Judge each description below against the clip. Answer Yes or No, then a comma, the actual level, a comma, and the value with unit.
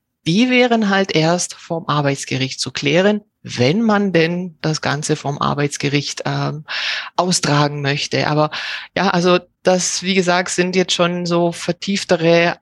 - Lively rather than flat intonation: No, average, 4.0 semitones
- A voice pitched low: No, medium, 170 Hz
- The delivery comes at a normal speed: Yes, average, 140 wpm